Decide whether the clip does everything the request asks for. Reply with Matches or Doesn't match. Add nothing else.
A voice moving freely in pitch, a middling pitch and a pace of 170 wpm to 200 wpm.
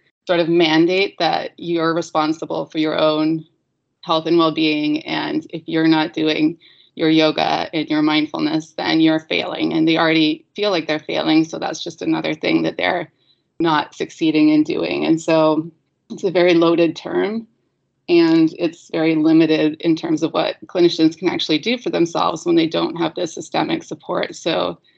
Matches